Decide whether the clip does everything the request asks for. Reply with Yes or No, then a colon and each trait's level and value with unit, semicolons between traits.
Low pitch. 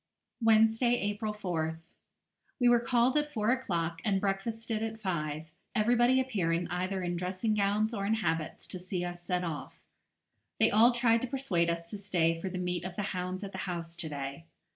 No: high, 195 Hz